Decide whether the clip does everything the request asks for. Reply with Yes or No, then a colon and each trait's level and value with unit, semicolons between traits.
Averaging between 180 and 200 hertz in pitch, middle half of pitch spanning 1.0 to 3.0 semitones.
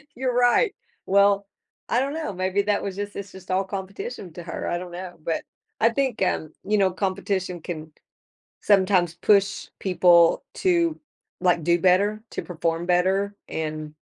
Yes: high, 190 Hz; narrow, 2.6 semitones